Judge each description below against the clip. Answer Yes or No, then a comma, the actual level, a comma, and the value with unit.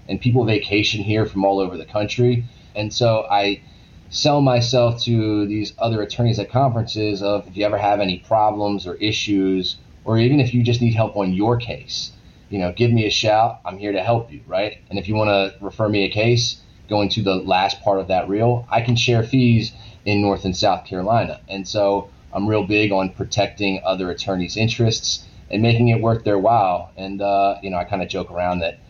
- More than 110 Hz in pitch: No, low, 105 Hz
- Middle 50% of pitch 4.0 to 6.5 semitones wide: No, average, 2.9 semitones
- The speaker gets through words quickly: Yes, fast, 215 wpm